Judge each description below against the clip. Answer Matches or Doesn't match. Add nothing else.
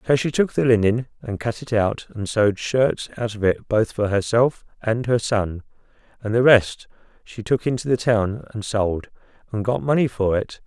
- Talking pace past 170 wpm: Matches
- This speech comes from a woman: Doesn't match